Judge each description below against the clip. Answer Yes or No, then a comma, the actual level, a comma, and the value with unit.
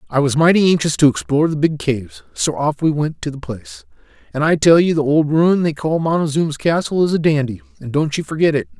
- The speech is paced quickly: Yes, fast, 240 wpm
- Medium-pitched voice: Yes, medium, 150 Hz